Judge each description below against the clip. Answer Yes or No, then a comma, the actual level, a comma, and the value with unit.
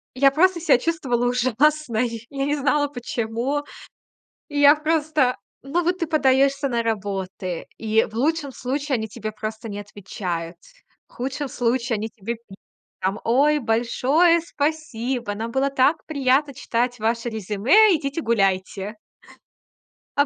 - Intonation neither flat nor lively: Yes, average, 4.7 semitones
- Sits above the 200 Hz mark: Yes, very high, 250 Hz